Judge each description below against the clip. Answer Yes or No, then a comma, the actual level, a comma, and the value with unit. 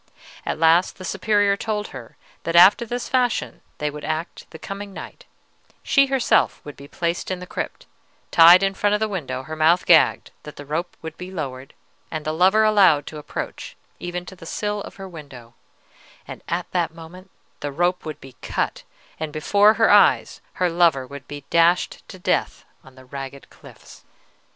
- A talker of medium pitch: Yes, medium, 170 Hz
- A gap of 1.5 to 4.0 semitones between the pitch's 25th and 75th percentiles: No, average, 4.5 semitones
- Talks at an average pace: Yes, average, 185 wpm